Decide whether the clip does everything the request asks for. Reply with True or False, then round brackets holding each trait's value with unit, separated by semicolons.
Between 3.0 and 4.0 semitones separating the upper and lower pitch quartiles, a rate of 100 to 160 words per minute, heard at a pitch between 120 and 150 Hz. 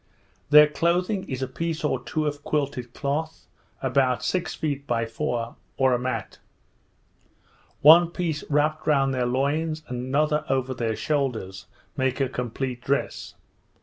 True (3.4 semitones; 145 wpm; 140 Hz)